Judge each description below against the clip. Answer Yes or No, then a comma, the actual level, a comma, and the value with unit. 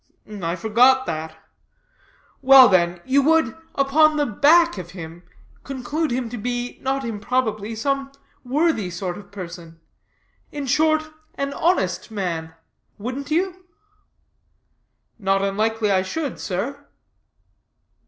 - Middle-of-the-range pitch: No, high, 240 Hz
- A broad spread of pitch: Yes, wide, 6.5 semitones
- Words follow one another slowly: Yes, slow, 115 wpm